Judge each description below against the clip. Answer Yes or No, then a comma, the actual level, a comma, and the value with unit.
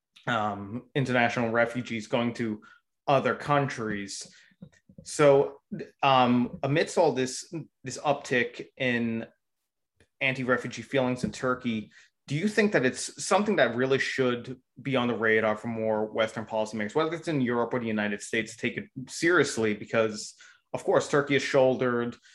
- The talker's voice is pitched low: Yes, low, 125 Hz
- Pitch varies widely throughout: No, average, 3.1 semitones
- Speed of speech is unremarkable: No, fast, 145 wpm